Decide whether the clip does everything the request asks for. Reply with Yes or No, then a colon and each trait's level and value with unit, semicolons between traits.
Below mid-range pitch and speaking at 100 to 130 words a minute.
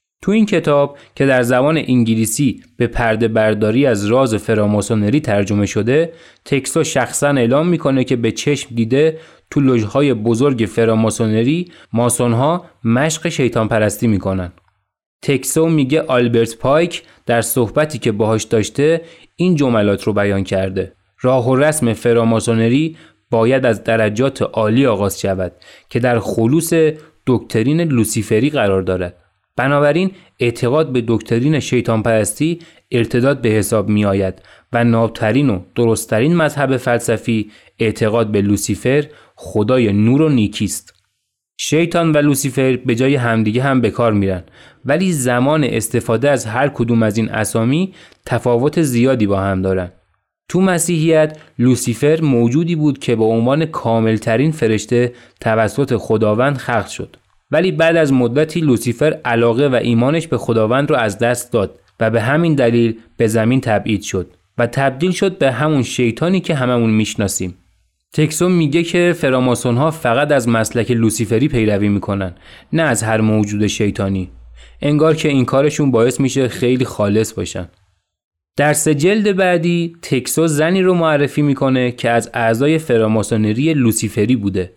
No: low, 120 Hz; average, 140 wpm